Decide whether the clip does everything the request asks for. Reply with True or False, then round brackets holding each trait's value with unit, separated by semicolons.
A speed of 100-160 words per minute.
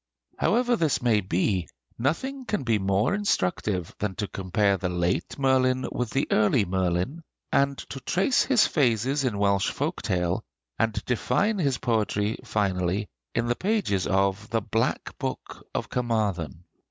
True (150 wpm)